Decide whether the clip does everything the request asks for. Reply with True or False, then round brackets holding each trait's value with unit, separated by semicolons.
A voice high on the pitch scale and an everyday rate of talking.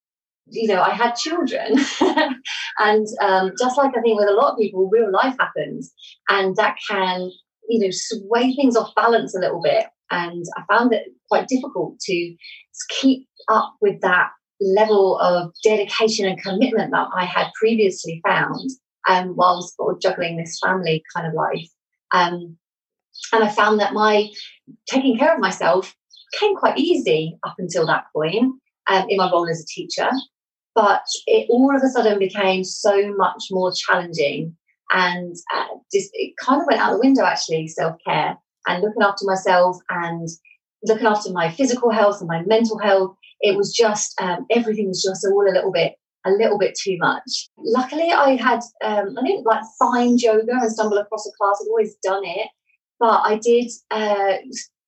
True (210 Hz; 175 wpm)